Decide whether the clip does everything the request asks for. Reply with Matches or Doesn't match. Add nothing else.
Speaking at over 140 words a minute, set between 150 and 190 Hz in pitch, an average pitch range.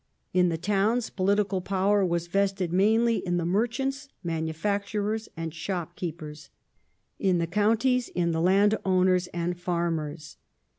Doesn't match